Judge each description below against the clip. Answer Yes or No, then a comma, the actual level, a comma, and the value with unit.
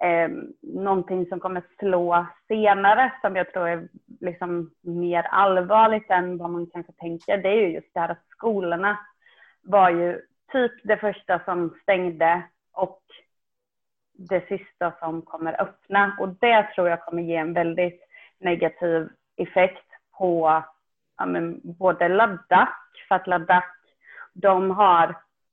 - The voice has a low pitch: No, medium, 180 Hz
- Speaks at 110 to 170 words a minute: Yes, average, 135 wpm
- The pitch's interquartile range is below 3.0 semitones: Yes, narrow, 2.5 semitones